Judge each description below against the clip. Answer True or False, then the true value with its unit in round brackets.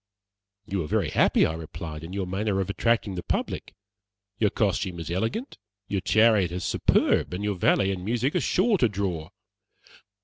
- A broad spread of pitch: False (3.5 semitones)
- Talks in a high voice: False (95 Hz)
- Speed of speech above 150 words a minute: True (175 wpm)